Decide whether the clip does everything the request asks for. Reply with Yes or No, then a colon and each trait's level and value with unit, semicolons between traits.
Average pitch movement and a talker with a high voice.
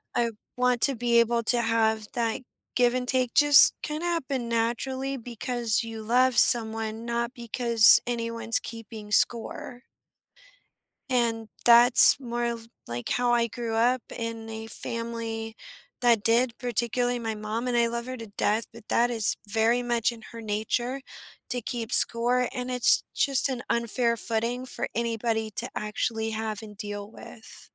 No: narrow, 1.5 semitones; high, 235 Hz